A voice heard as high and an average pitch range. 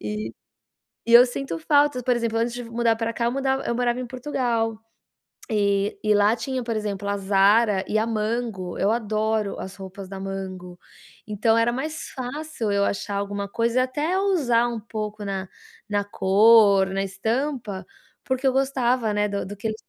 Yes: high, 220 Hz; average, 3.4 semitones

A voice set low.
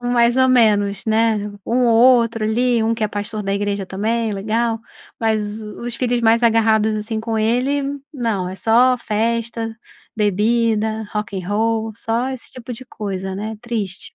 No: high, 225 Hz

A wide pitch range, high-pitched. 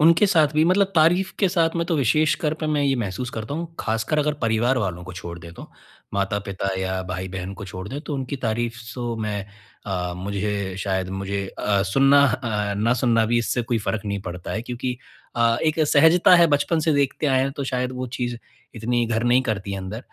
No: wide, 6.1 semitones; low, 120 Hz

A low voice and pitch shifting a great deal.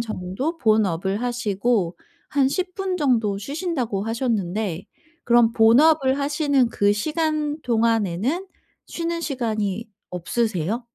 No: high, 235 Hz; wide, 5.9 semitones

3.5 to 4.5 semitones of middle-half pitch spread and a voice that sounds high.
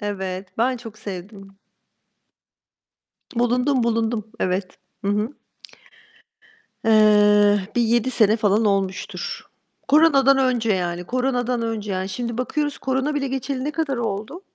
Yes: average, 4.0 semitones; high, 225 Hz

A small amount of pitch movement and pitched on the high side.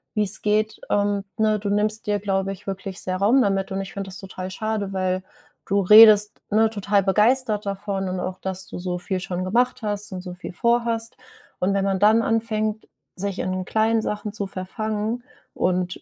Yes: narrow, 2.3 semitones; high, 200 Hz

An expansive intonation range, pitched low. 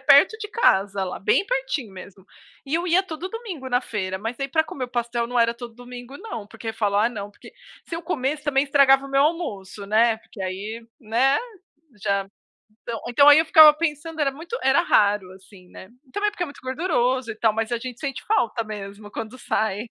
No: wide, 5.9 semitones; high, 245 Hz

